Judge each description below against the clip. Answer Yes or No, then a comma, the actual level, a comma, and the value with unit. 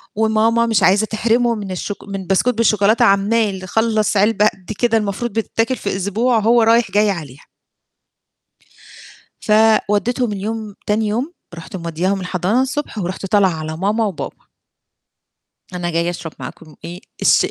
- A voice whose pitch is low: No, high, 210 Hz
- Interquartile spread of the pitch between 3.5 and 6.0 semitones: No, average, 3.0 semitones